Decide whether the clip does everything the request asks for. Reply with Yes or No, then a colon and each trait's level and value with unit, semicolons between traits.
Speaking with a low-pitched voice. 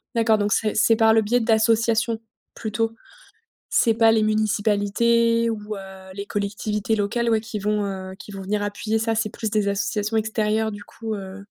No: high, 215 Hz